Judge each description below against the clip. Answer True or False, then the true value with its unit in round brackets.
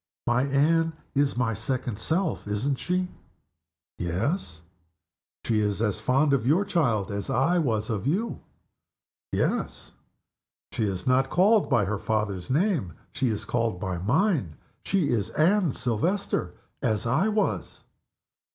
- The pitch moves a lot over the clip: True (7.5 semitones)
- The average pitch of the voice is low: True (125 Hz)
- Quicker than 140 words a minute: False (135 wpm)